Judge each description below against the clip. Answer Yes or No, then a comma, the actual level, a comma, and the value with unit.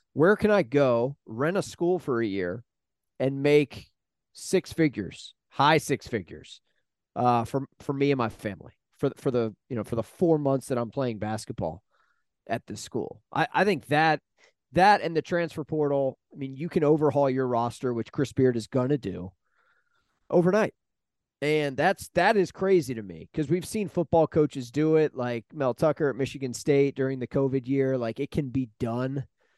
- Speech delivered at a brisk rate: No, average, 185 wpm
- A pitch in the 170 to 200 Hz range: No, low, 135 Hz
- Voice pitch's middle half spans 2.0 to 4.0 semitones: No, average, 4.4 semitones